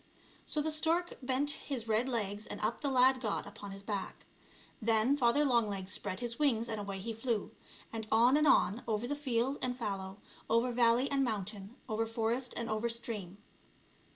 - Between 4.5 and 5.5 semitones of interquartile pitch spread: No, average, 3.3 semitones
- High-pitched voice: Yes, high, 230 Hz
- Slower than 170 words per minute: No, average, 180 wpm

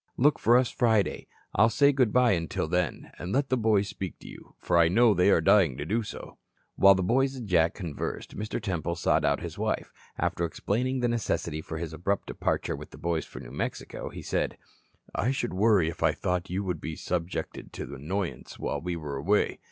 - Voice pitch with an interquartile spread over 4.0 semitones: Yes, wide, 5.4 semitones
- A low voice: Yes, very low, 95 Hz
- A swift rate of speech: Yes, fast, 215 wpm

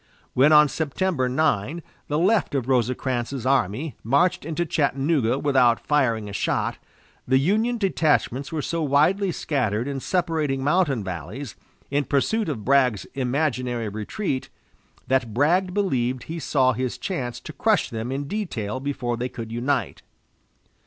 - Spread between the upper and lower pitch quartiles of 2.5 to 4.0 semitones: No, average, 4.5 semitones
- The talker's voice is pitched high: No, low, 135 Hz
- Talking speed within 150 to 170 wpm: No, average, 140 wpm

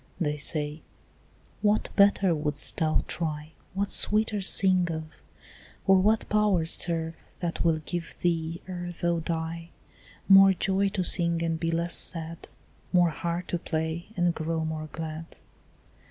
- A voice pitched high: No, medium, 170 Hz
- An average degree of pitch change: No, narrow, 2.3 semitones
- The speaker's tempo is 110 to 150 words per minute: Yes, average, 140 wpm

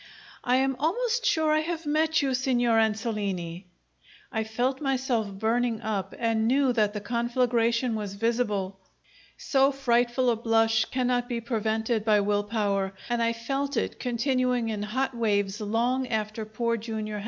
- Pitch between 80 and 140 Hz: No, high, 230 Hz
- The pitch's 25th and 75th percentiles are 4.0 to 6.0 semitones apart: No, average, 3.0 semitones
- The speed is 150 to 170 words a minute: Yes, average, 155 wpm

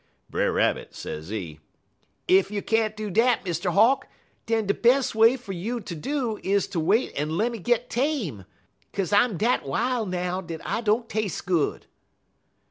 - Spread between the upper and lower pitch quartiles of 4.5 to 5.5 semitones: Yes, average, 4.8 semitones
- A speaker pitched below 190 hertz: No, high, 210 Hz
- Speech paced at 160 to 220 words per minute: Yes, average, 165 wpm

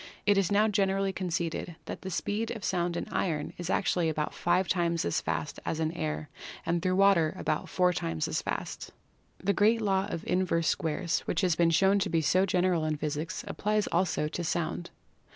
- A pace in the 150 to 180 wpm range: No, average, 195 wpm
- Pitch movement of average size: Yes, average, 3.0 semitones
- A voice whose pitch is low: No, medium, 175 Hz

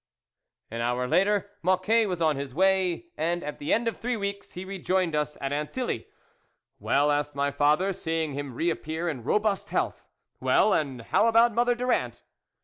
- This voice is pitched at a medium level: Yes, medium, 170 Hz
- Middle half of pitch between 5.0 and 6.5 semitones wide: Yes, wide, 5.6 semitones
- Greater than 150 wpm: Yes, average, 180 wpm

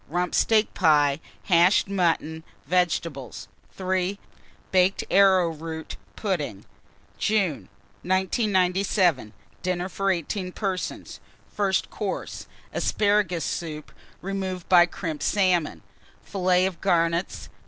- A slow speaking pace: Yes, slow, 90 wpm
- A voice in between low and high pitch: Yes, medium, 180 Hz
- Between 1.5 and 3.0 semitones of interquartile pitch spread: Yes, narrow, 2.6 semitones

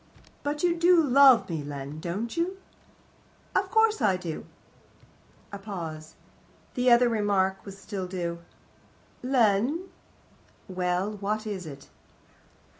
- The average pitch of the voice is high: Yes, high, 205 Hz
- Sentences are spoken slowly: Yes, slow, 120 wpm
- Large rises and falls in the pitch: Yes, wide, 6.2 semitones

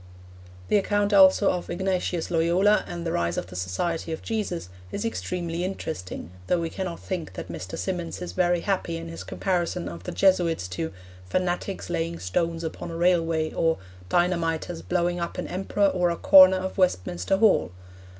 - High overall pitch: No, medium, 175 Hz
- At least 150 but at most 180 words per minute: Yes, average, 170 wpm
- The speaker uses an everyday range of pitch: No, narrow, 2.2 semitones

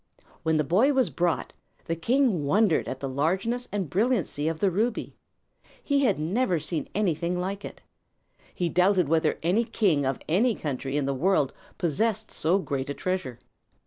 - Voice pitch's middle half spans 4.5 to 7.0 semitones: Yes, wide, 5.6 semitones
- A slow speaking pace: No, average, 170 wpm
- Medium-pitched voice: Yes, medium, 180 Hz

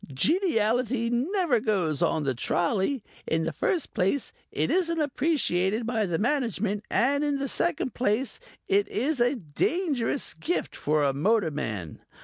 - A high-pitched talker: Yes, high, 230 Hz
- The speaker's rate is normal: Yes, average, 145 wpm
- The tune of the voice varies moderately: No, wide, 8.1 semitones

